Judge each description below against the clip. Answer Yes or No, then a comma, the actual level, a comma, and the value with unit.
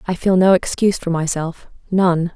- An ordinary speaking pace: Yes, average, 180 wpm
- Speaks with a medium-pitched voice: Yes, medium, 175 Hz